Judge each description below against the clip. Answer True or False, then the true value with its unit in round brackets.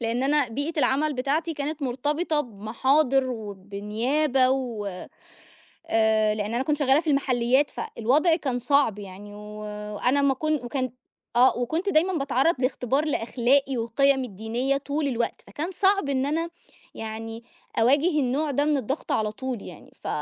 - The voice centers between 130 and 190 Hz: False (260 Hz)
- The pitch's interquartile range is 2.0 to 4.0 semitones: False (4.4 semitones)